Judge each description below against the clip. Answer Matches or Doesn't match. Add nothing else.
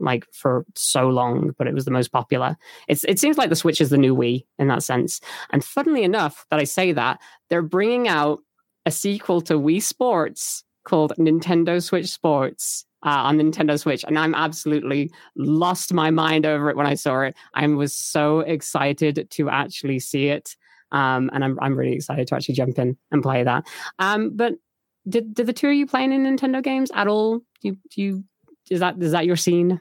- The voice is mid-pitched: Matches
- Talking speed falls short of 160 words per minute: Doesn't match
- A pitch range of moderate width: Matches